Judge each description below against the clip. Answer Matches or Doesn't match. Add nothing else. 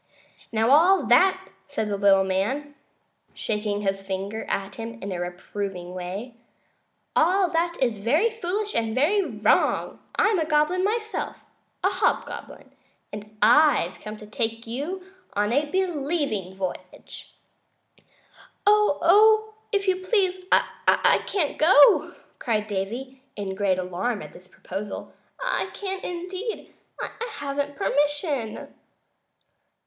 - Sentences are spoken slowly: Matches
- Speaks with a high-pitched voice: Matches